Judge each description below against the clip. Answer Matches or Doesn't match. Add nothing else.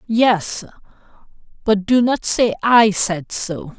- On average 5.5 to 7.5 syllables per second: Doesn't match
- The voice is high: Matches